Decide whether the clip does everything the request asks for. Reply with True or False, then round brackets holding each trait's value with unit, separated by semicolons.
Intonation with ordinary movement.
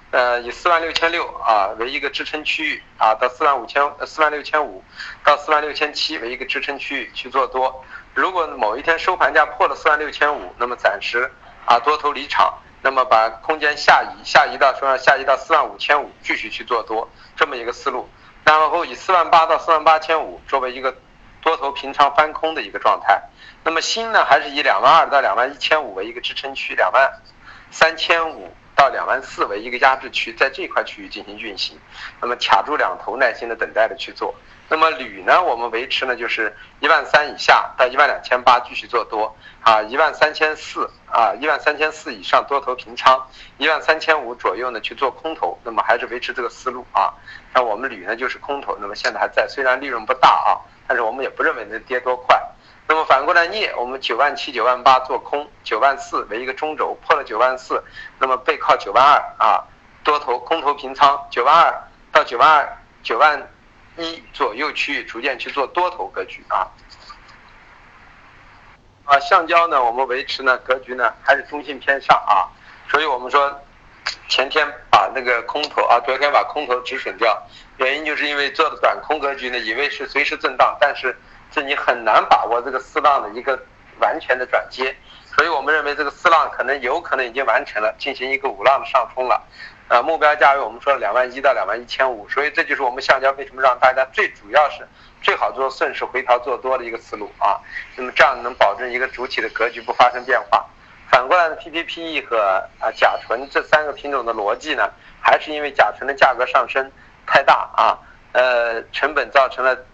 True (3.4 semitones)